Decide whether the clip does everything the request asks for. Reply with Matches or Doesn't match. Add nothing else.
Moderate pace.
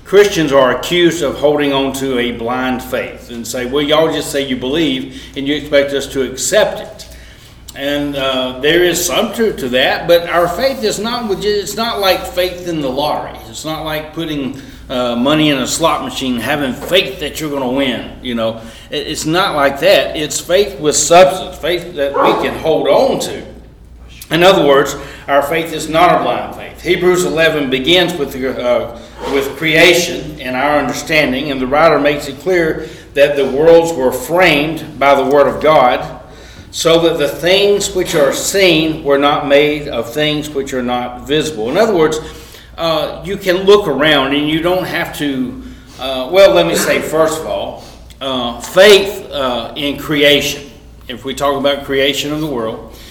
Matches